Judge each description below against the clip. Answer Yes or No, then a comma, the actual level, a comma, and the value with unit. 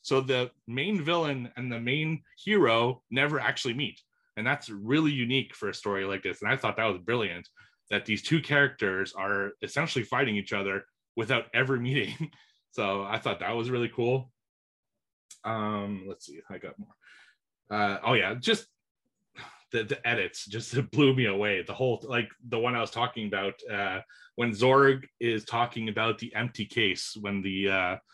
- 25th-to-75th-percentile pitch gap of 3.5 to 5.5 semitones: Yes, average, 4.4 semitones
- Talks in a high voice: No, low, 120 Hz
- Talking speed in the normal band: Yes, average, 180 wpm